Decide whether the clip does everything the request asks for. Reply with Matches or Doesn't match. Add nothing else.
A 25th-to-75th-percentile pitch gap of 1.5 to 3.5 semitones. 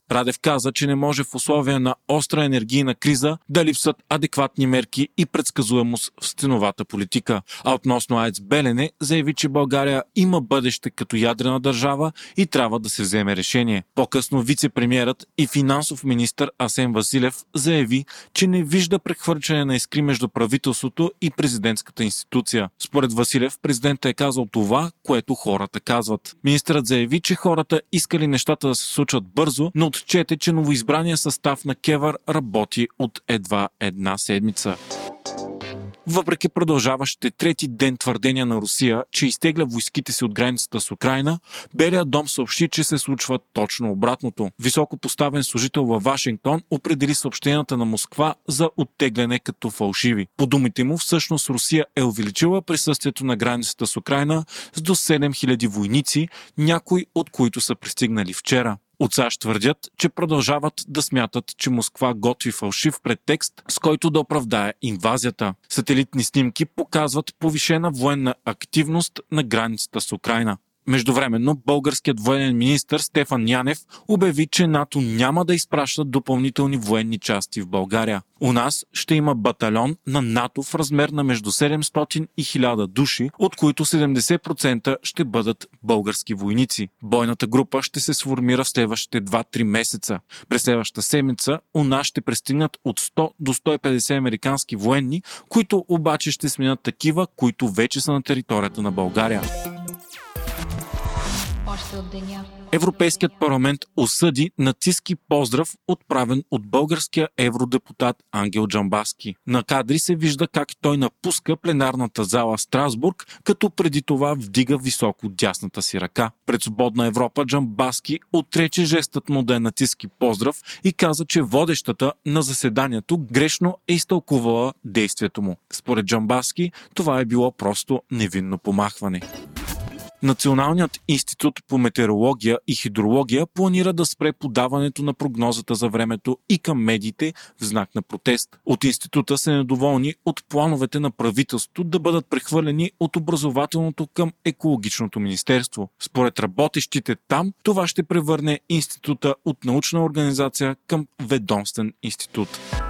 Doesn't match